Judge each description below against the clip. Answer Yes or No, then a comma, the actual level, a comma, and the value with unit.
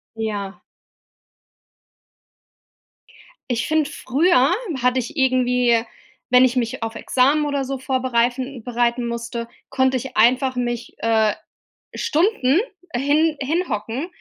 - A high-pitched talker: Yes, very high, 255 Hz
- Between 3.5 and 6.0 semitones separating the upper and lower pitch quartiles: No, narrow, 2.5 semitones